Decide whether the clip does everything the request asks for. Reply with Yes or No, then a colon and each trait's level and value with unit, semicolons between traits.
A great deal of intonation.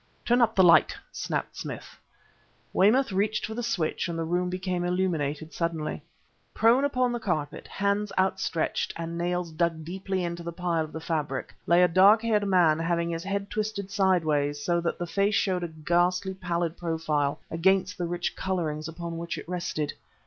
No: average, 2.8 semitones